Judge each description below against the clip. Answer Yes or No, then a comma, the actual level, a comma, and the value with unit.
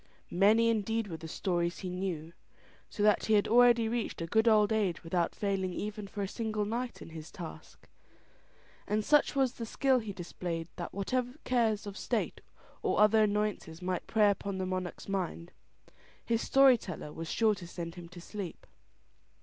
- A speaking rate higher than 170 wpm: Yes, average, 180 wpm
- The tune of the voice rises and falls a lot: No, average, 4.0 semitones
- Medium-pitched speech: No, high, 205 Hz